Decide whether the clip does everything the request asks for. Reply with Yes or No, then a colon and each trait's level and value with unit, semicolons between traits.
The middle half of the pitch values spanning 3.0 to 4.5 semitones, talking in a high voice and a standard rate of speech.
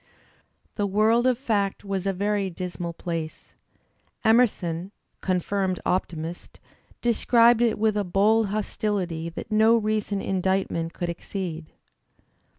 No: average, 3.5 semitones; high, 195 Hz; slow, 115 wpm